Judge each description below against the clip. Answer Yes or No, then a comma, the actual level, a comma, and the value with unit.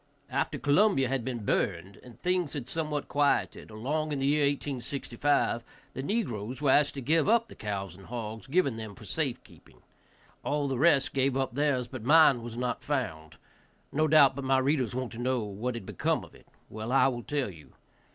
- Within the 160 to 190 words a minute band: No, average, 200 wpm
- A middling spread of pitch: Yes, average, 3.8 semitones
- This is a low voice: Yes, low, 130 Hz